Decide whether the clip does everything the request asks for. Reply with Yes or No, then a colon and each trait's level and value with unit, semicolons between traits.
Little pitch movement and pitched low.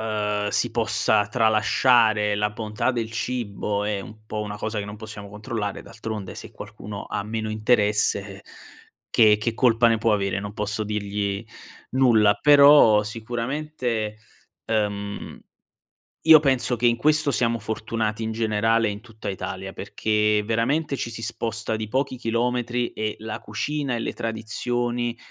Yes: narrow, 2.1 semitones; low, 110 Hz